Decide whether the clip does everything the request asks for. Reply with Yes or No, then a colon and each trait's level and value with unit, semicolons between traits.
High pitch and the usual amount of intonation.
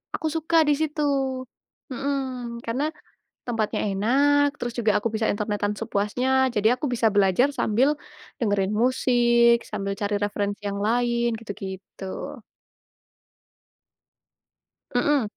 Yes: high, 235 Hz; average, 4.2 semitones